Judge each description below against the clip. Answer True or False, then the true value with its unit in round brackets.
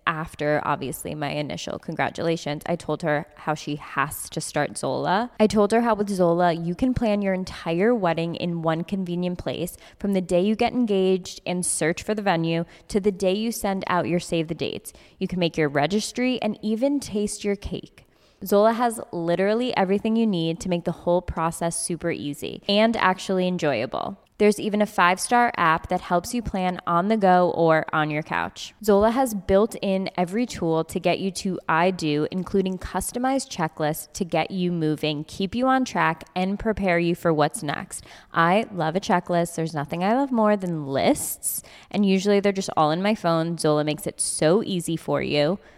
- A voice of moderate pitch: True (180 Hz)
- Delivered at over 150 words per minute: True (195 wpm)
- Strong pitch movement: False (3.9 semitones)